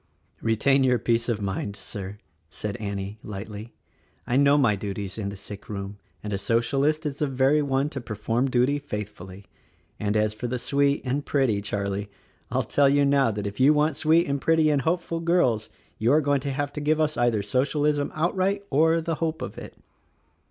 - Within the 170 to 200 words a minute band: Yes, average, 195 wpm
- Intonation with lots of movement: Yes, wide, 5.7 semitones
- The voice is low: Yes, low, 130 Hz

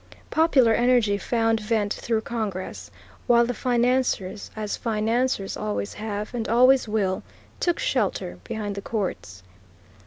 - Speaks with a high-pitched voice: Yes, high, 220 Hz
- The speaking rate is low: Yes, slow, 125 wpm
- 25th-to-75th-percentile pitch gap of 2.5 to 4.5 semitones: Yes, average, 3.1 semitones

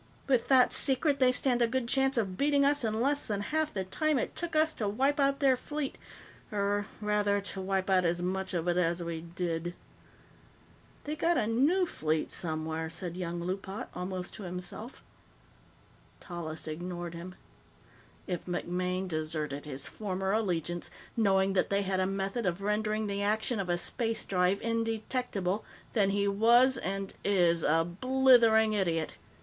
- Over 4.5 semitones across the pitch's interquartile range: Yes, average, 5.0 semitones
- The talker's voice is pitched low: No, high, 200 Hz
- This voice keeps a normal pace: Yes, average, 165 wpm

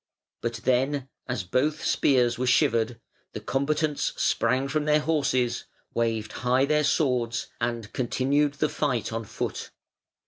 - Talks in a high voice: No, low, 130 Hz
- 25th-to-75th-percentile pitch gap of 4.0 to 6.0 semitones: No, average, 3.6 semitones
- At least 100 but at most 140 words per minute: Yes, slow, 135 wpm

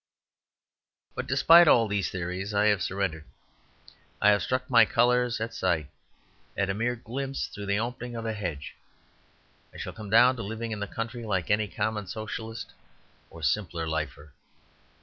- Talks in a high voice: No, low, 110 Hz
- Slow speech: No, average, 165 wpm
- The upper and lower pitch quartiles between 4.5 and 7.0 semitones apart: No, average, 3.5 semitones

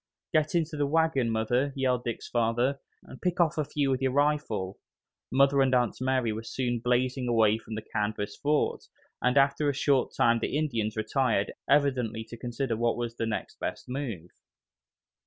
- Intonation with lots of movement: No, average, 3.6 semitones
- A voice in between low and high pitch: No, low, 125 Hz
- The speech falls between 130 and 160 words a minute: No, average, 175 wpm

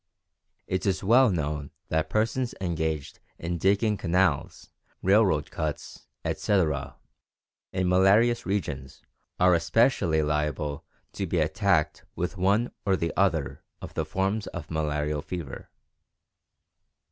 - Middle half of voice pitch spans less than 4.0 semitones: No, average, 4.4 semitones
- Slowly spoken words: Yes, slow, 115 wpm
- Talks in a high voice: No, very low, 90 Hz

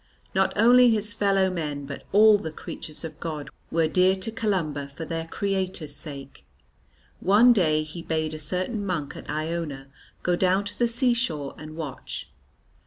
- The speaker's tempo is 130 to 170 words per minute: Yes, average, 165 wpm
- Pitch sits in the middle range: Yes, medium, 170 Hz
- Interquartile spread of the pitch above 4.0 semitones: Yes, average, 4.7 semitones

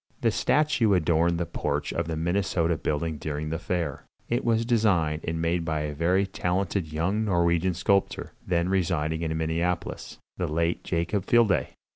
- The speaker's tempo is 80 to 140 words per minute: No, average, 160 wpm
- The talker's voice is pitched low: Yes, very low, 85 Hz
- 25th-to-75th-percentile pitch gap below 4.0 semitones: Yes, average, 3.0 semitones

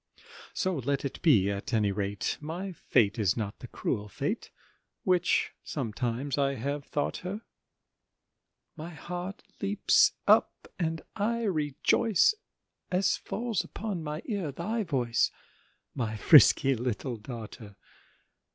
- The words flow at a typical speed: No, slow, 125 wpm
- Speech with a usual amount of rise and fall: No, wide, 7.7 semitones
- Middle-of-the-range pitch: Yes, medium, 145 Hz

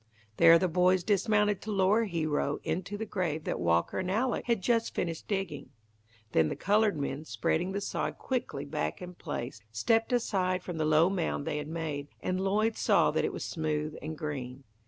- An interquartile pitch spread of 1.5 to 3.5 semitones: No, average, 5.0 semitones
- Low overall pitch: No, medium, 180 Hz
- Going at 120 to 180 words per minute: No, average, 190 wpm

